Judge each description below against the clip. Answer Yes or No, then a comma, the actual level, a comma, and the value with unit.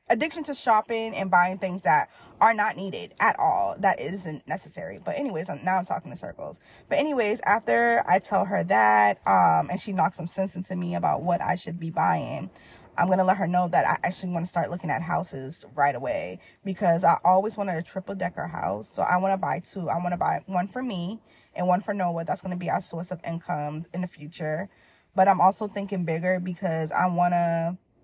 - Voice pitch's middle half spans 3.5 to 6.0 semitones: No, narrow, 2.6 semitones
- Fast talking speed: Yes, fast, 225 wpm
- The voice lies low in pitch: No, medium, 180 Hz